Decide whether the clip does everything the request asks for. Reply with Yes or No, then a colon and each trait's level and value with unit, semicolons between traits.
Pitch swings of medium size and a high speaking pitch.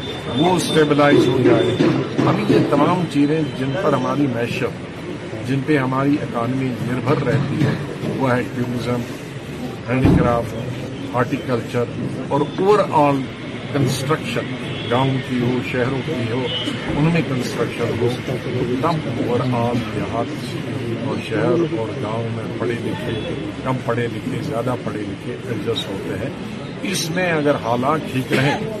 No: average, 3.2 semitones; low, 130 Hz